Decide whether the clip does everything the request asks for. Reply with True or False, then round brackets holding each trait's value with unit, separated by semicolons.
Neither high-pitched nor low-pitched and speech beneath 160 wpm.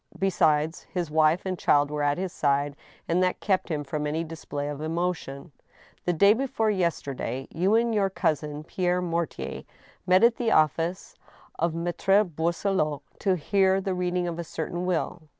False (170 Hz; 170 wpm)